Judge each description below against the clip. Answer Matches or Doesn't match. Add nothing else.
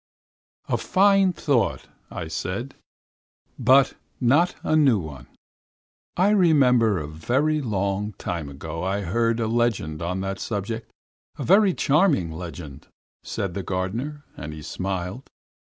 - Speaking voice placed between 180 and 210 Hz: Doesn't match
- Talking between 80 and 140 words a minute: Matches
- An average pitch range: Doesn't match